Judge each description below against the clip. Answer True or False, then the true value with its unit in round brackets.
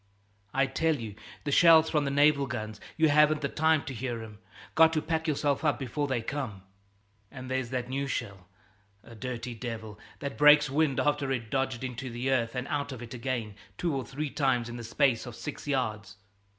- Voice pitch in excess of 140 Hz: False (130 Hz)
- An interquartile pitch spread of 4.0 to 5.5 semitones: False (3.6 semitones)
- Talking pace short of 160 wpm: False (205 wpm)